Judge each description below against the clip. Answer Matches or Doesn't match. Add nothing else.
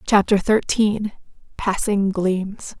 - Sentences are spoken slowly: Matches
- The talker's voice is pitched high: Matches